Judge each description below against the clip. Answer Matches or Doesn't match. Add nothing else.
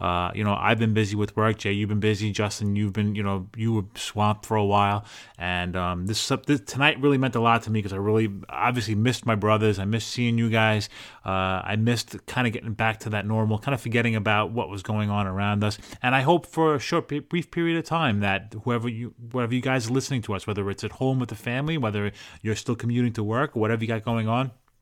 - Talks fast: Matches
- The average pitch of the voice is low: Matches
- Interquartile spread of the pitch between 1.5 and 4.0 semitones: Matches